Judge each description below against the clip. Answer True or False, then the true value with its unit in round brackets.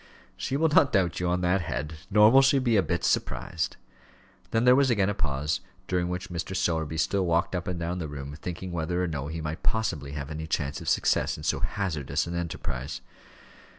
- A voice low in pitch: True (85 Hz)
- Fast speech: True (215 wpm)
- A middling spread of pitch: True (3.7 semitones)